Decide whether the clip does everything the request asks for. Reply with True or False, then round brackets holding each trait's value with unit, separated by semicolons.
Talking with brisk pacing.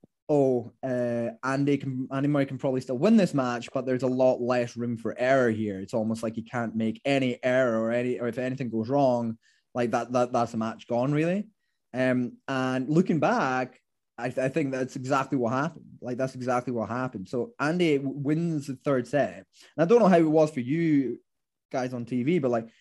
True (215 wpm)